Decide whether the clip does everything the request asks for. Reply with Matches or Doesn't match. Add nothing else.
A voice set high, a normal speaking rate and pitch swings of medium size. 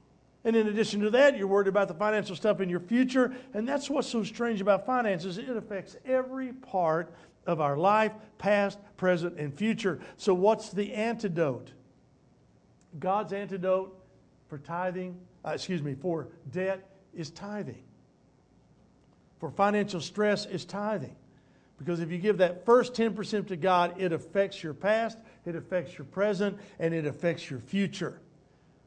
Matches